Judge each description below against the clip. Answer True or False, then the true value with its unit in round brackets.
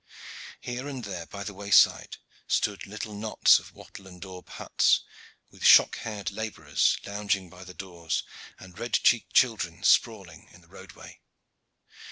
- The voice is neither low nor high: False (100 Hz)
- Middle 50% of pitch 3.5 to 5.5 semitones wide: False (3.0 semitones)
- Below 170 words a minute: True (150 wpm)